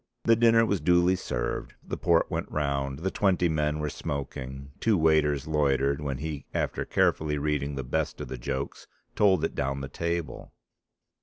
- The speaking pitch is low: Yes, very low, 75 Hz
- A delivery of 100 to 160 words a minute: No, average, 170 wpm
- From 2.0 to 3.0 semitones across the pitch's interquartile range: No, average, 3.8 semitones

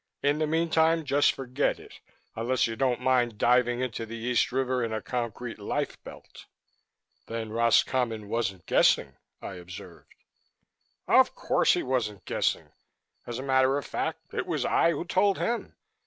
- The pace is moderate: Yes, average, 155 wpm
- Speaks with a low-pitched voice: Yes, low, 125 Hz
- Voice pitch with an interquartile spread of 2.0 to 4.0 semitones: Yes, average, 3.0 semitones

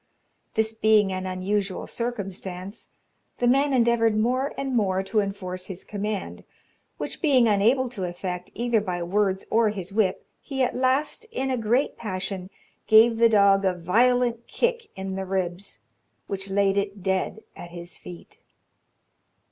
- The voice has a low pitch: No, high, 205 Hz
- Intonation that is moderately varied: Yes, average, 3.9 semitones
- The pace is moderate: Yes, average, 150 wpm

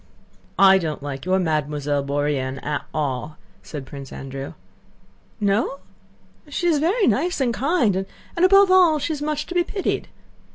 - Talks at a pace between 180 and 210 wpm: No, average, 150 wpm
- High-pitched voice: Yes, high, 195 Hz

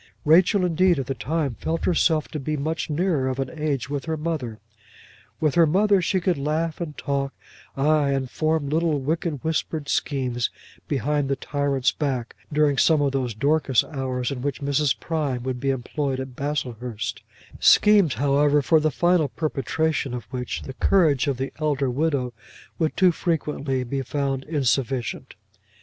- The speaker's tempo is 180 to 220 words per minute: No, average, 165 wpm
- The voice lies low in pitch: No, medium, 145 Hz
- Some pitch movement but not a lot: Yes, average, 3.1 semitones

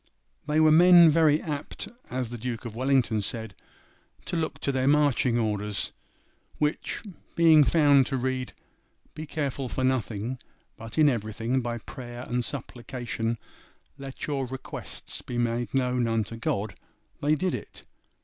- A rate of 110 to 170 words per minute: Yes, average, 145 wpm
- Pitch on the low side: Yes, low, 130 Hz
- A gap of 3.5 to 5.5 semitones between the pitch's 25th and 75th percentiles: Yes, average, 3.9 semitones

